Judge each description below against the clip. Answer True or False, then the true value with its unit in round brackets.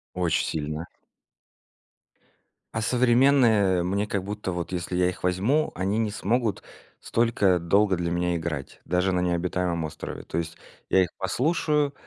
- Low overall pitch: True (95 Hz)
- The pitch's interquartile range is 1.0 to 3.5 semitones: False (4.2 semitones)